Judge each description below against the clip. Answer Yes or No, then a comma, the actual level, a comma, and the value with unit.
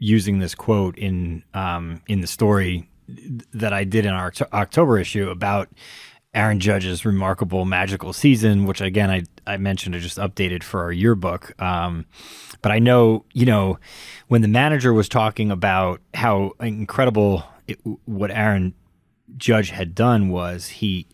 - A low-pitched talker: Yes, low, 100 Hz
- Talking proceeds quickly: No, average, 155 wpm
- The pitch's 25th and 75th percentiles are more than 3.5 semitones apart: No, average, 3.2 semitones